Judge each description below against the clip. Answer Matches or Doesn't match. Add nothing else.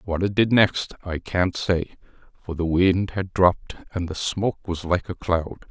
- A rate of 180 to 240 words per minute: Matches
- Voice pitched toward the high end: Doesn't match